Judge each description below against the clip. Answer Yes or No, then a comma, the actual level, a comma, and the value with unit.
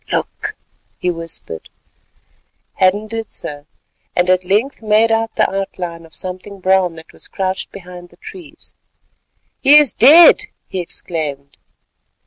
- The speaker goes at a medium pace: No, slow, 130 wpm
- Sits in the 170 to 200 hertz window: Yes, high, 190 Hz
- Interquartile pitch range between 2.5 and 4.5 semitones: Yes, average, 4.2 semitones